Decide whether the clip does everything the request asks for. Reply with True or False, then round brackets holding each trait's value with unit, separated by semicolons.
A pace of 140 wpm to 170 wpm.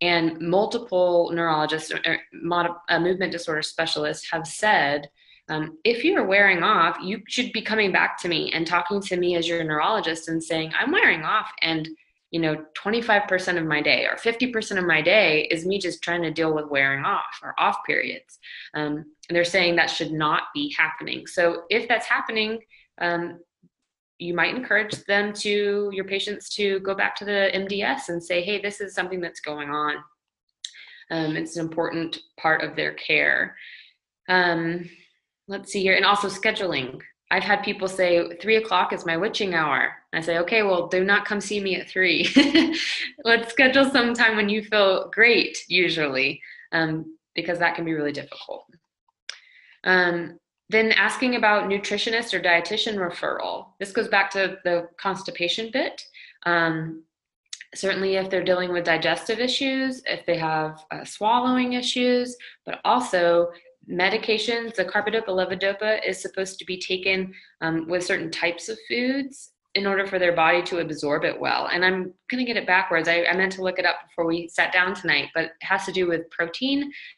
False (180 wpm)